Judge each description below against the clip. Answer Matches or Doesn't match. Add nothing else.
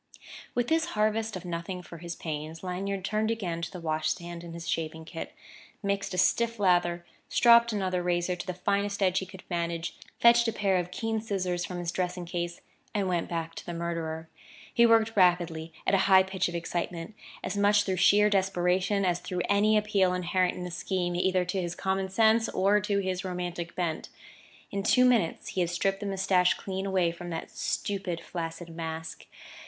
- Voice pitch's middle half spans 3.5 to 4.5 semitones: Doesn't match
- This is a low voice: Doesn't match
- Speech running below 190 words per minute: Doesn't match